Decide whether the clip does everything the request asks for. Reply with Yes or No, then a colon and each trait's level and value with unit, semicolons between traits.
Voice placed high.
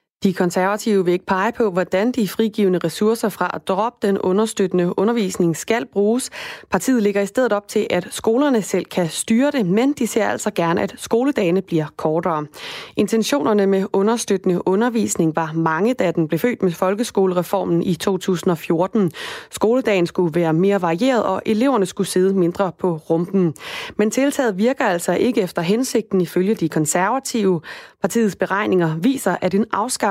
Yes: high, 195 Hz